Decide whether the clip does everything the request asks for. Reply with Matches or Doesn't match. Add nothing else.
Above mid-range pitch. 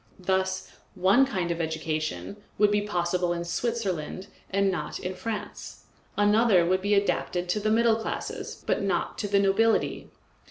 Matches